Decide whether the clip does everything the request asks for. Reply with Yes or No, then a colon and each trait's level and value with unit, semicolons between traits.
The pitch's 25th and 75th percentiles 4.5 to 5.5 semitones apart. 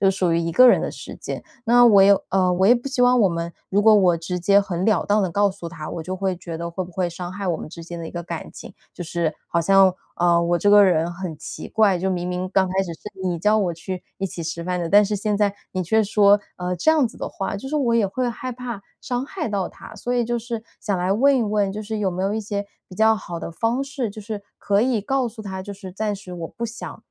No: average, 3.7 semitones